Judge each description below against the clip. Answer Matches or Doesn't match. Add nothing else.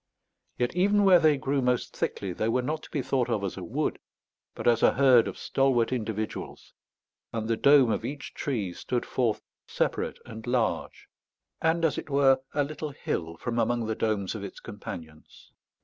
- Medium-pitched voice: Doesn't match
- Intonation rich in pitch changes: Doesn't match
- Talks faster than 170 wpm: Matches